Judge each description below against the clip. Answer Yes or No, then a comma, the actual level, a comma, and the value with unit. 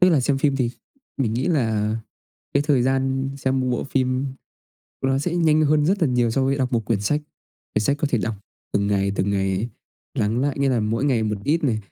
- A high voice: No, low, 130 Hz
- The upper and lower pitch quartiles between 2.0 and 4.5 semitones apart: Yes, average, 4.0 semitones